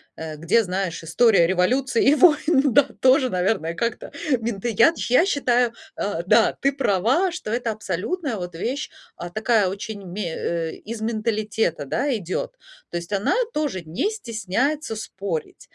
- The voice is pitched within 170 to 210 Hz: No, high, 220 Hz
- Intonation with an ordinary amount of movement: No, wide, 6.0 semitones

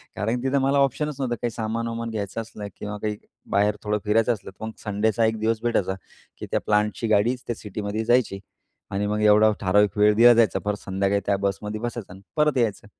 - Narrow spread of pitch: Yes, narrow, 2.1 semitones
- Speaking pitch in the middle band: No, low, 110 Hz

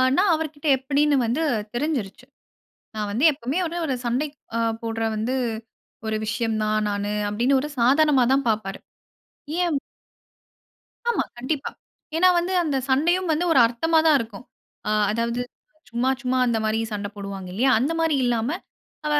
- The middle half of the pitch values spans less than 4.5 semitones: No, average, 5.2 semitones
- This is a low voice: No, very high, 255 Hz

